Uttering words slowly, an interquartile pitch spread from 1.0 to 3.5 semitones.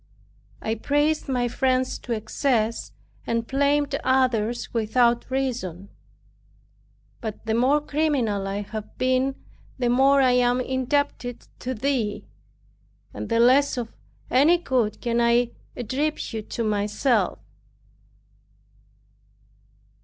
Yes: slow, 110 wpm; average, 2.9 semitones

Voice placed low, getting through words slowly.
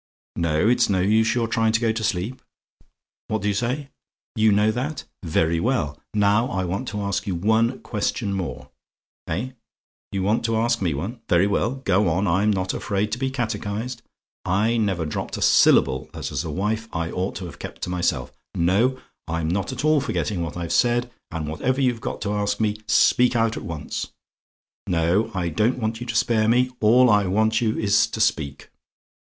No: low, 105 Hz; average, 195 wpm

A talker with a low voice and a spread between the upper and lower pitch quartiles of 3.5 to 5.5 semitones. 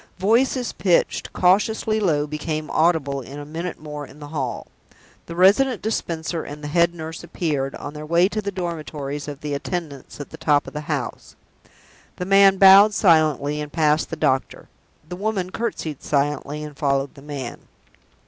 No: medium, 155 Hz; average, 3.8 semitones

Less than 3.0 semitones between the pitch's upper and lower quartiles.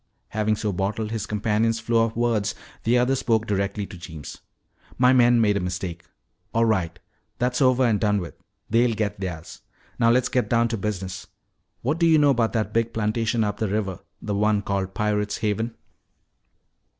Yes: narrow, 2.6 semitones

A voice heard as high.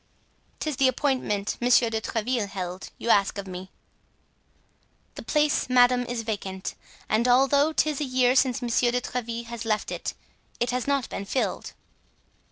Yes: high, 245 Hz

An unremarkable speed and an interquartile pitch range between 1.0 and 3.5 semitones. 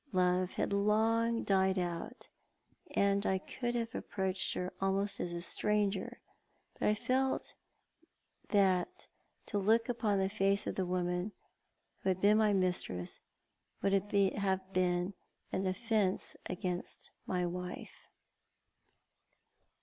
No: slow, 120 wpm; narrow, 2.4 semitones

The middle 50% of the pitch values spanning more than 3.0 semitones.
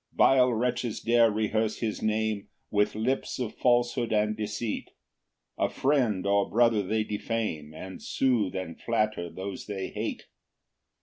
No: narrow, 2.6 semitones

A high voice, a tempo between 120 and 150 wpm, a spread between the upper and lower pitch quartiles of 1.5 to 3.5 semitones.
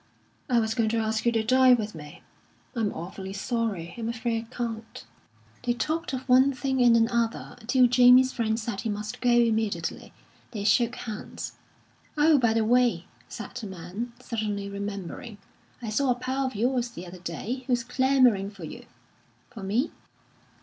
No: high, 230 Hz; average, 170 wpm; average, 3.1 semitones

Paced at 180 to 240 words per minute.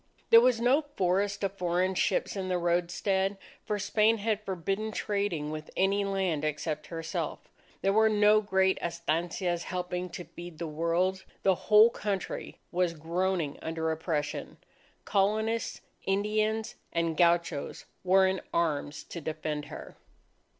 No: slow, 135 wpm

